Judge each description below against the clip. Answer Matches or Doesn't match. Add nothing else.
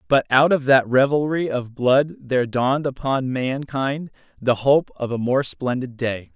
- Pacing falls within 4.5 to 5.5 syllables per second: Doesn't match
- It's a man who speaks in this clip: Matches